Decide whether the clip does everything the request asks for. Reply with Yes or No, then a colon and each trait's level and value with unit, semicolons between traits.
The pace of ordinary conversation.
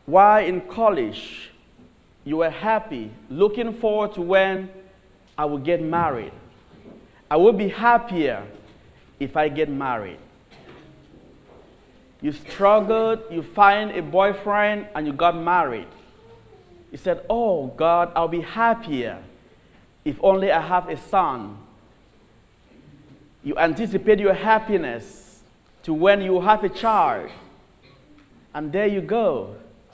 No: slow, 120 wpm